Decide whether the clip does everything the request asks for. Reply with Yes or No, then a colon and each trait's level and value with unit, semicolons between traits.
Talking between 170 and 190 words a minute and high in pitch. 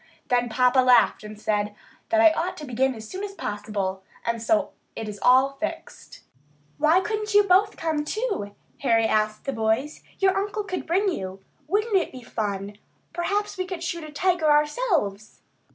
Yes: average, 175 wpm; very high, 295 Hz